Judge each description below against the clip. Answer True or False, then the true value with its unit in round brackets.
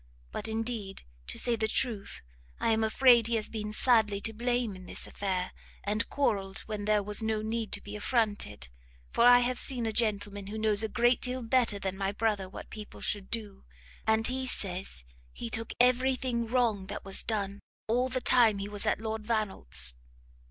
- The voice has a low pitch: False (220 Hz)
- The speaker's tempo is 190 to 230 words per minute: True (195 wpm)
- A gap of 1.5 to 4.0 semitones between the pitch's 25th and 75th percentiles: True (2.8 semitones)